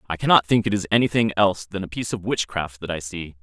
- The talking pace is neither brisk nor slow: No, fast, 265 wpm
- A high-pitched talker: No, very low, 95 Hz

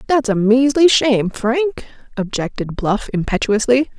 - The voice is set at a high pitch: Yes, high, 235 Hz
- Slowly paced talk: Yes, slow, 120 wpm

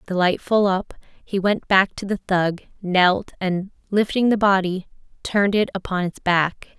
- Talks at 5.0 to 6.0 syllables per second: No, 4.5 syllables/s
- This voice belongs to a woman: Yes, female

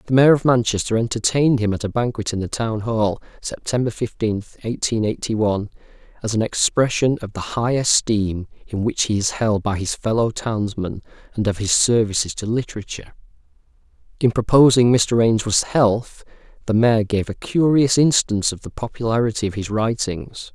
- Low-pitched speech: Yes, low, 110 Hz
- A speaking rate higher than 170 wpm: No, average, 165 wpm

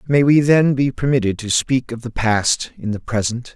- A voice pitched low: Yes, low, 125 Hz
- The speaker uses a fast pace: Yes, fast, 220 wpm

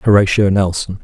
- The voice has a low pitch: Yes, low, 100 Hz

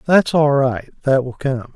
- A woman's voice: No, male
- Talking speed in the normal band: Yes, average, 170 wpm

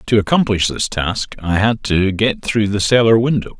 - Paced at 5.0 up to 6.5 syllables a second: No, 4.7 syllables/s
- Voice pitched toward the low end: Yes, low, 105 Hz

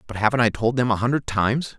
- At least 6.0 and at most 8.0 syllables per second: Yes, 6.8 syllables/s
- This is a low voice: Yes, low, 115 Hz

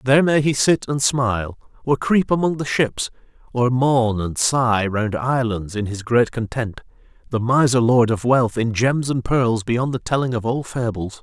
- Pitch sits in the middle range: No, low, 120 Hz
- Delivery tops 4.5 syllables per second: No, 4.4 syllables/s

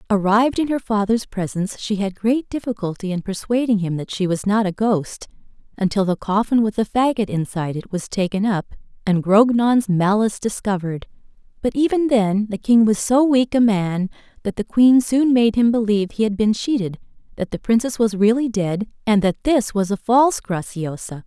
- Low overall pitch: No, high, 215 Hz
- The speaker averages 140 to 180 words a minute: No, average, 190 wpm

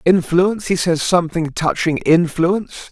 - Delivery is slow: Yes, slow, 125 wpm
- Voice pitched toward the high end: No, medium, 170 Hz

